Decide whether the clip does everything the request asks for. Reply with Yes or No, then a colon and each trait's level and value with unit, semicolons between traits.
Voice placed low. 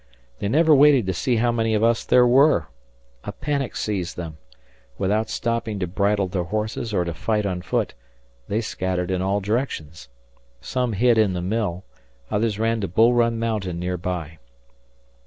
Yes: low, 105 Hz